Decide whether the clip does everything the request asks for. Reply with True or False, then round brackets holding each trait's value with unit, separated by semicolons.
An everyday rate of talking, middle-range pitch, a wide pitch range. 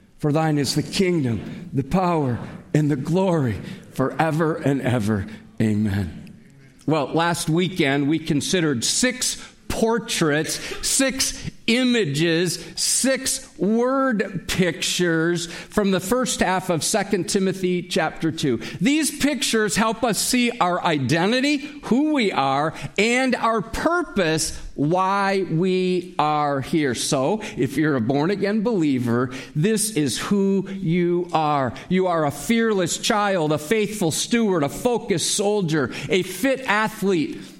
False (125 wpm; 180 Hz; 6.0 semitones)